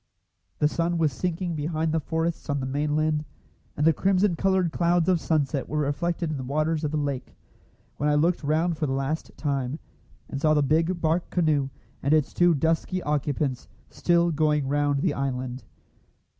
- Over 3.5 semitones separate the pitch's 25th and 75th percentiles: No, narrow, 2.6 semitones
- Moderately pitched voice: Yes, medium, 155 Hz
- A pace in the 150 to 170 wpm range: No, average, 180 wpm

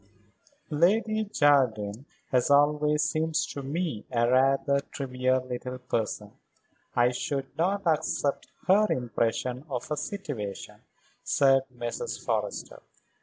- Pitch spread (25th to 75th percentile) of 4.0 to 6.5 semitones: No, average, 3.5 semitones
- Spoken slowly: Yes, slow, 110 wpm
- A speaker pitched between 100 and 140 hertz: Yes, low, 135 Hz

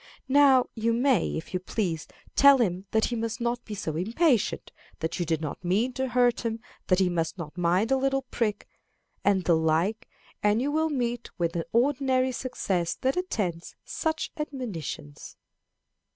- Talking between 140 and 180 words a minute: Yes, average, 170 wpm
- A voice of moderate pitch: No, high, 225 Hz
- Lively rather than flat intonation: Yes, wide, 6.6 semitones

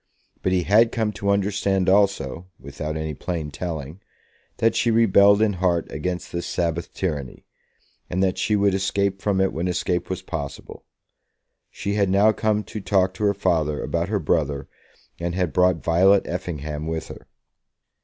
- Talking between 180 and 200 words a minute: No, average, 165 wpm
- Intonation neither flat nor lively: Yes, average, 3.3 semitones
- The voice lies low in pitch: Yes, very low, 90 Hz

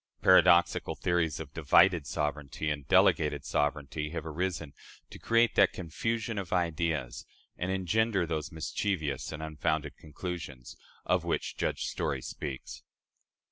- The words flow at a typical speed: No, slow, 125 wpm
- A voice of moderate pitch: No, very low, 80 Hz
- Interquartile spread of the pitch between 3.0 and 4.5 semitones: Yes, average, 3.6 semitones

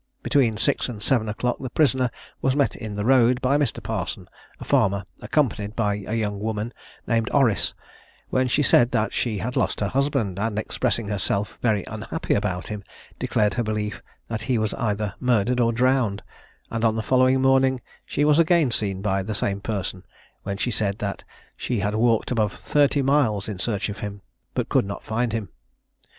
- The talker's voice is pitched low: Yes, low, 110 Hz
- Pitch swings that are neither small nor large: Yes, average, 3.7 semitones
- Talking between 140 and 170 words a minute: No, average, 190 wpm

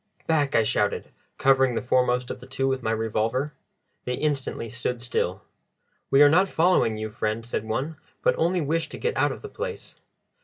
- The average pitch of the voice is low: Yes, low, 130 Hz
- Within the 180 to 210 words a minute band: Yes, average, 190 wpm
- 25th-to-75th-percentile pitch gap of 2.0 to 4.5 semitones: No, average, 5.0 semitones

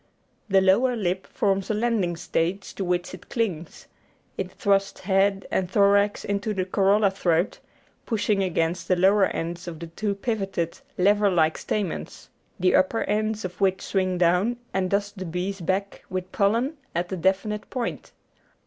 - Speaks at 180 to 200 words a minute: No, average, 160 wpm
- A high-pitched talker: Yes, high, 195 Hz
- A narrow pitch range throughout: Yes, narrow, 2.3 semitones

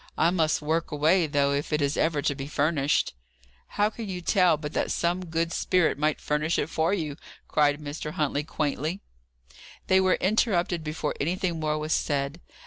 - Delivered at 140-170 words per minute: No, average, 180 wpm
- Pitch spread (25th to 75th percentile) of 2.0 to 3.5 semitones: Yes, average, 2.8 semitones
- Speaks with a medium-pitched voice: Yes, medium, 155 Hz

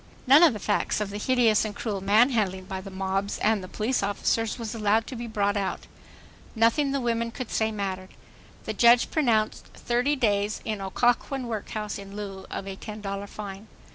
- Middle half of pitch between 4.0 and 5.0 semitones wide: No, average, 2.9 semitones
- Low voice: No, high, 215 Hz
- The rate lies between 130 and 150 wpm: No, average, 180 wpm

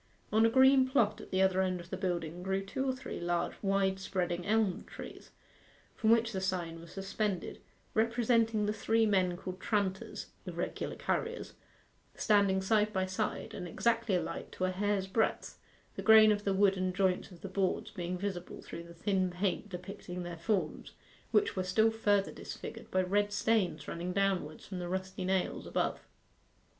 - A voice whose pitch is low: No, high, 190 Hz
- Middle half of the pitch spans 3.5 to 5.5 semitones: No, average, 2.8 semitones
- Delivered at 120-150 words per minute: No, average, 175 wpm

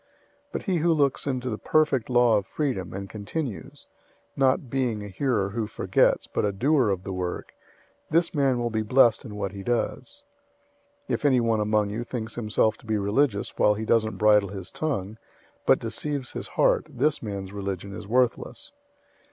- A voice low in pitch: Yes, low, 115 Hz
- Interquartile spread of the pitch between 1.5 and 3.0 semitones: No, average, 4.6 semitones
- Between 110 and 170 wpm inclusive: No, average, 185 wpm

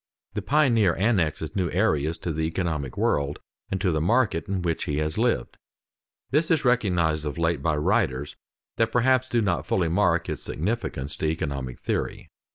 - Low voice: Yes, very low, 85 Hz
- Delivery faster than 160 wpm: Yes, average, 170 wpm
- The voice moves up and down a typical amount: No, wide, 6.3 semitones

